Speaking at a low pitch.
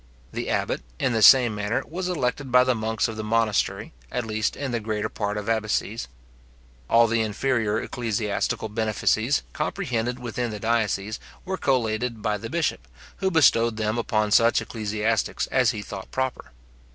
Yes: low, 115 Hz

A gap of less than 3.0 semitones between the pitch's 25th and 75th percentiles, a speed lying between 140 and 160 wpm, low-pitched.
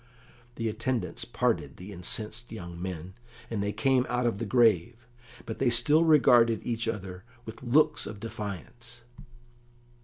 No: average, 3.4 semitones; average, 145 wpm; low, 115 Hz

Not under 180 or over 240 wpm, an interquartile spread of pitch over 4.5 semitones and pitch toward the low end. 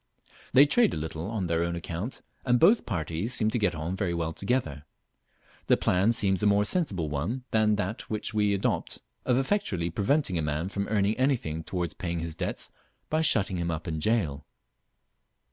Yes: average, 190 wpm; average, 5.2 semitones; very low, 95 Hz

